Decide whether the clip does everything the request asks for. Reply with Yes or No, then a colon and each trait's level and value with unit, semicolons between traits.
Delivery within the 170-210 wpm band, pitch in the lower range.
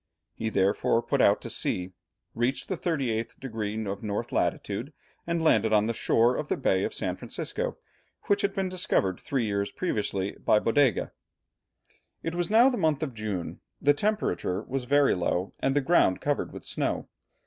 Yes: average, 175 wpm; low, 120 Hz